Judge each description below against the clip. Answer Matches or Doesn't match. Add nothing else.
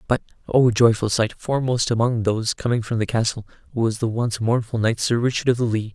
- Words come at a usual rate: Matches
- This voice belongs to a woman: Doesn't match